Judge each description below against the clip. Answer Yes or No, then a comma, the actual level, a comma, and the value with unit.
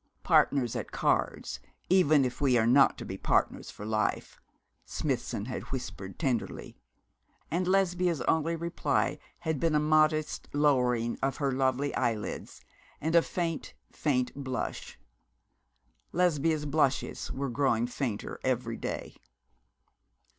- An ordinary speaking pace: No, slow, 120 wpm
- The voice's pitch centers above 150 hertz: No, medium, 140 Hz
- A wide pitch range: No, average, 4.2 semitones